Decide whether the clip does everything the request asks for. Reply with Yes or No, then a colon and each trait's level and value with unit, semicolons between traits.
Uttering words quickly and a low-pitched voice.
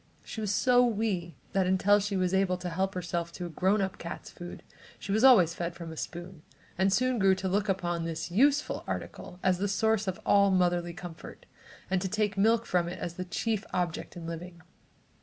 No: fast, 210 wpm; medium, 185 Hz